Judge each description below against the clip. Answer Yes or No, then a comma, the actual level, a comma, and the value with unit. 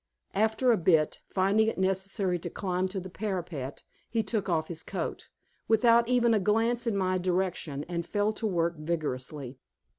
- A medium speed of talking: Yes, average, 170 wpm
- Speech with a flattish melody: No, average, 4.3 semitones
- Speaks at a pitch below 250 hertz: Yes, high, 190 Hz